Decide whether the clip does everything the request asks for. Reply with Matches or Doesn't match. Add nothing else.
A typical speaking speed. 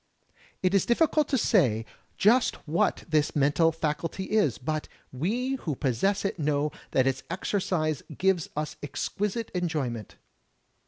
Doesn't match